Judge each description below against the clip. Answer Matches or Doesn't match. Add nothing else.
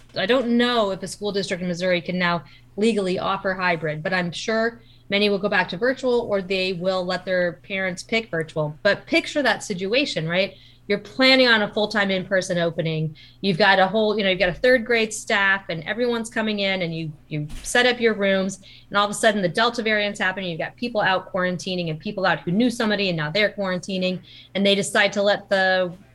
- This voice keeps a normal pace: Doesn't match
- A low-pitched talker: Doesn't match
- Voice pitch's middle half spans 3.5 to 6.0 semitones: Doesn't match